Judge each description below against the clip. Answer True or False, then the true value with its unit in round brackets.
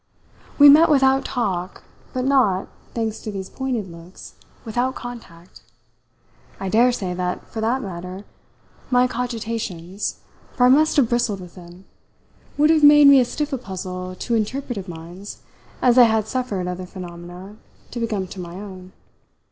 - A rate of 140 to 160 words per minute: True (155 wpm)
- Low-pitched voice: False (215 Hz)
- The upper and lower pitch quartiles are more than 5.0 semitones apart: True (5.5 semitones)